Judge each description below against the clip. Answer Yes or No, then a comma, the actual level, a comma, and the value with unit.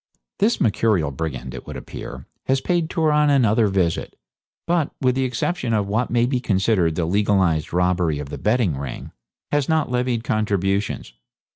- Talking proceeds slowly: No, average, 160 wpm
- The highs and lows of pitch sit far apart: Yes, wide, 6.4 semitones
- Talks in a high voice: No, low, 110 Hz